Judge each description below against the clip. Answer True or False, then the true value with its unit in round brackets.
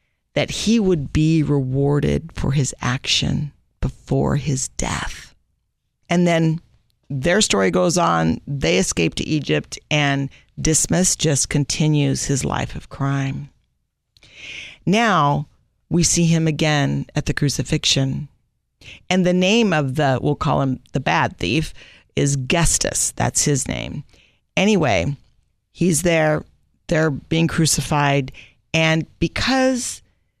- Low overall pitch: False (145 Hz)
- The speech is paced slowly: True (120 wpm)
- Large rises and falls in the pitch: False (3.2 semitones)